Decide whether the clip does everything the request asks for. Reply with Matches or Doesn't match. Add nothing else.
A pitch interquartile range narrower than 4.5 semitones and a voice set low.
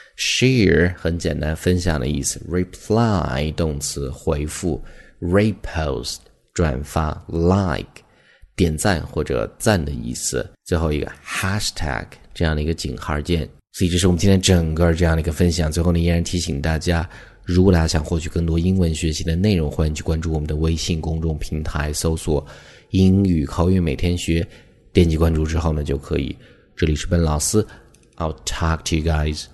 Matches